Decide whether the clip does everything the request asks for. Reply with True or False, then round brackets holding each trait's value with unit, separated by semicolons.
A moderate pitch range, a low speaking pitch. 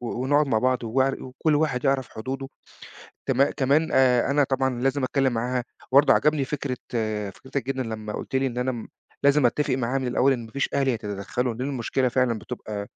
False (2.0 semitones; 130 Hz)